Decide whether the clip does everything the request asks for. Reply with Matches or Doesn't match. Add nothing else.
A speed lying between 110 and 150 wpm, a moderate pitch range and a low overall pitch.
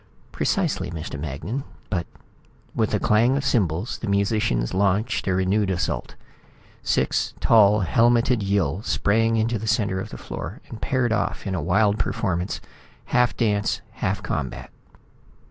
Matches